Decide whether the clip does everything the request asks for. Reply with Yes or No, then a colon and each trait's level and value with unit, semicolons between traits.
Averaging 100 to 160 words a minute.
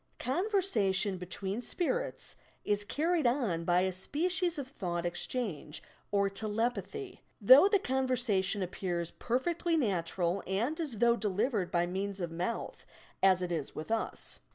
Yes: average, 140 wpm